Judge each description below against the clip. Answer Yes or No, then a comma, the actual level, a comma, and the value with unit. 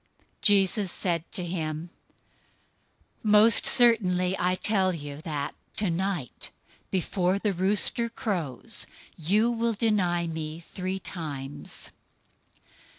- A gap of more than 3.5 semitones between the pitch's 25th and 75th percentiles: Yes, average, 3.9 semitones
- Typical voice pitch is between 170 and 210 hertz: Yes, medium, 185 Hz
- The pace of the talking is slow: Yes, slow, 100 wpm